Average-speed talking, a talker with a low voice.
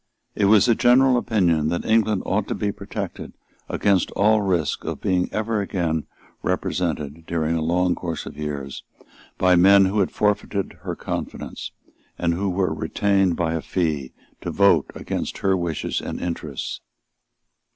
Yes: average, 155 wpm; very low, 90 Hz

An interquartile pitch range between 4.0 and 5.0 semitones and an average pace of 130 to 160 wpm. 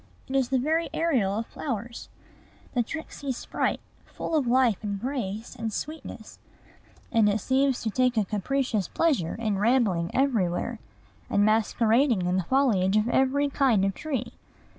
Yes: average, 4.7 semitones; average, 155 wpm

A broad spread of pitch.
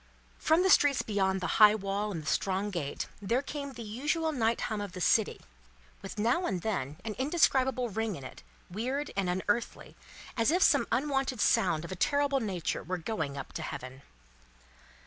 Yes: wide, 6.2 semitones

